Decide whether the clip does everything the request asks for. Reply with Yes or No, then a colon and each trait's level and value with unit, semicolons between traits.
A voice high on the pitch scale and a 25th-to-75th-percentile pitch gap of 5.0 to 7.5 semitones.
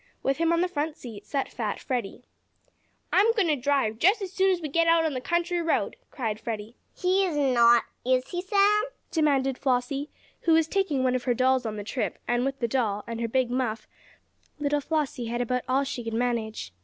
Yes: very high, 265 Hz; wide, 5.5 semitones